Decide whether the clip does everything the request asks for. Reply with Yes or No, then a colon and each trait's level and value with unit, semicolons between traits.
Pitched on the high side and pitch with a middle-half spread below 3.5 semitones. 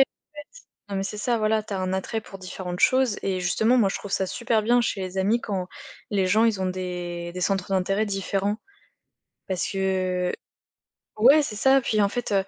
Yes: high, 195 Hz; average, 2.8 semitones